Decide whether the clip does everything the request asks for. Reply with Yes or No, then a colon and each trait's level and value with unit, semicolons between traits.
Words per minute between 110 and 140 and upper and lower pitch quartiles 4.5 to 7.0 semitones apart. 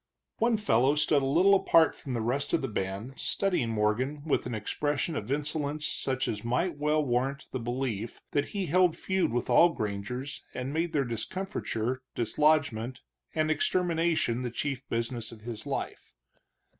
No: average, 165 wpm; average, 4.8 semitones